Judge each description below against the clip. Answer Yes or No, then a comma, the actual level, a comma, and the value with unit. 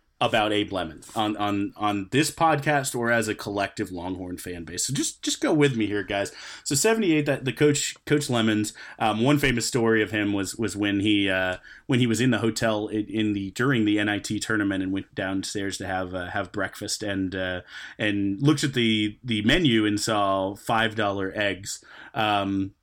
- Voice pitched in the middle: No, low, 105 Hz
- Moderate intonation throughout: Yes, average, 3.0 semitones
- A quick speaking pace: No, average, 195 wpm